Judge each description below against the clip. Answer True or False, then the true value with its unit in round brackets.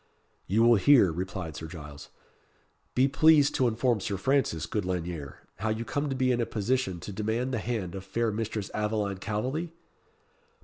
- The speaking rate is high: False (175 wpm)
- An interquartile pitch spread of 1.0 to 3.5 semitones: False (5.3 semitones)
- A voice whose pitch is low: True (110 Hz)